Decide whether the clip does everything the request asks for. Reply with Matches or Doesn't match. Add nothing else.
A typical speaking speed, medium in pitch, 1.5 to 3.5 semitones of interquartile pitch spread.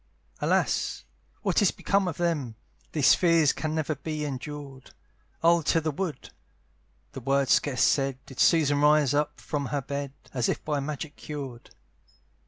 Matches